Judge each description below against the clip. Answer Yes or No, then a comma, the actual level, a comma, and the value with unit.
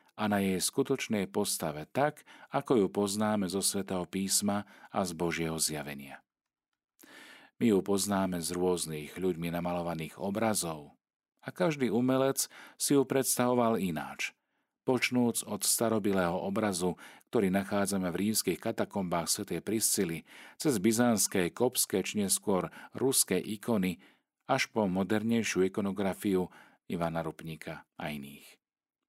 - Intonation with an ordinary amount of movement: Yes, average, 4.4 semitones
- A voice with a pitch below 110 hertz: Yes, low, 100 Hz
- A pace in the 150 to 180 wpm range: No, average, 120 wpm